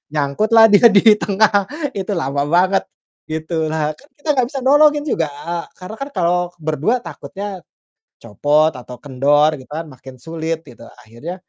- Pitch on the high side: No, medium, 165 Hz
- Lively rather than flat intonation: Yes, wide, 6.0 semitones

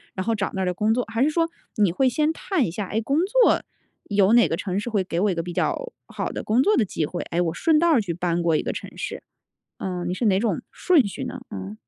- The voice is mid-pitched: No, high, 210 Hz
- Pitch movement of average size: No, wide, 6.7 semitones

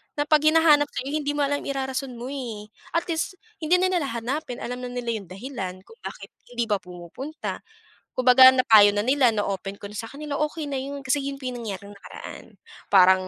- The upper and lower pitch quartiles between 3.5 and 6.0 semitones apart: Yes, wide, 5.4 semitones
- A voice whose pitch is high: Yes, very high, 255 Hz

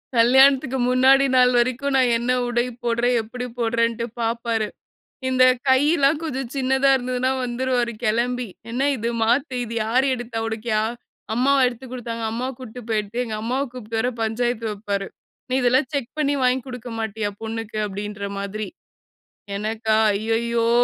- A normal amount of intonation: No, narrow, 2.3 semitones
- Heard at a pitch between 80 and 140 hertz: No, high, 240 Hz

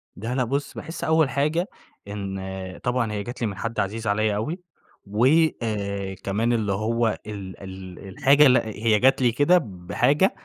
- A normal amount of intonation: Yes, average, 4.6 semitones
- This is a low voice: Yes, low, 110 Hz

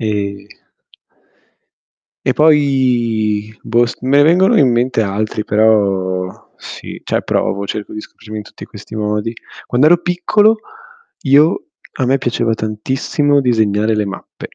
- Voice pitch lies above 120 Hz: No, low, 115 Hz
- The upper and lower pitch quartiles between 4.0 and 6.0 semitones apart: Yes, average, 4.4 semitones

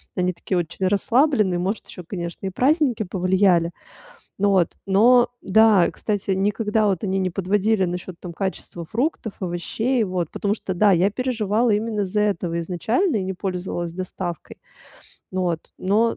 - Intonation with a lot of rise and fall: No, average, 3.2 semitones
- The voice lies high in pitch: Yes, high, 195 Hz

